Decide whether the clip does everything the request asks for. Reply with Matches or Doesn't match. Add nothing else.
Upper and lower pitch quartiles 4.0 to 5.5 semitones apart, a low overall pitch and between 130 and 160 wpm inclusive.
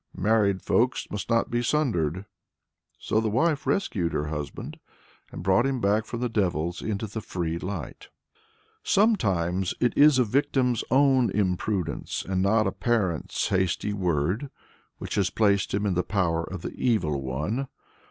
Matches